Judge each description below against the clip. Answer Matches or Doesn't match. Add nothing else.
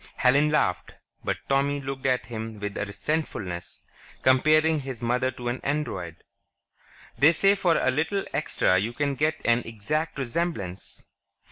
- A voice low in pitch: Matches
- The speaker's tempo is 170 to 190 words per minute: Doesn't match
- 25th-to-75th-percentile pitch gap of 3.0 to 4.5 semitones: Doesn't match